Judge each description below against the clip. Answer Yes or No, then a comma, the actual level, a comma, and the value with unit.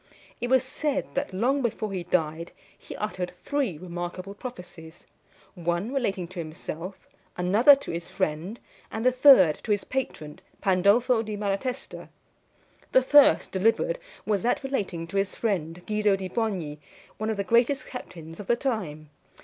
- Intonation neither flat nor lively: No, wide, 5.7 semitones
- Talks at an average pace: Yes, average, 155 wpm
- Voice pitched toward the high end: Yes, high, 200 Hz